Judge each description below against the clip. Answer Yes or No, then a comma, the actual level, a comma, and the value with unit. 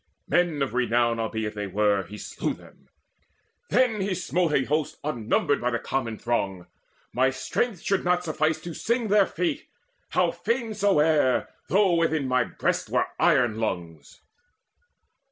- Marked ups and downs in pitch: Yes, wide, 7.9 semitones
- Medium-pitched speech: Yes, medium, 145 Hz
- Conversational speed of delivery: Yes, average, 150 wpm